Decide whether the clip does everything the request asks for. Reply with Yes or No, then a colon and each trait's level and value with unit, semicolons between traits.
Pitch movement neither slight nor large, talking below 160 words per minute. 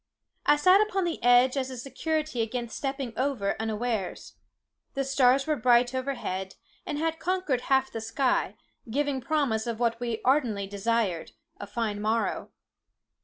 Yes: average, 3.8 semitones; average, 150 wpm